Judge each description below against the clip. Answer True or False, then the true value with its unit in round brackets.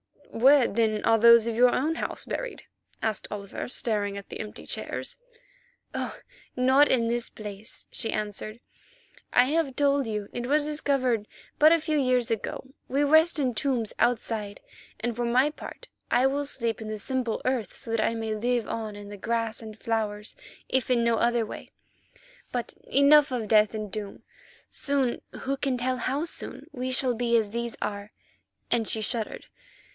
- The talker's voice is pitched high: True (235 Hz)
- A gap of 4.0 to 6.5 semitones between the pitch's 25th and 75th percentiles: False (3.4 semitones)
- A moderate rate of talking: True (175 wpm)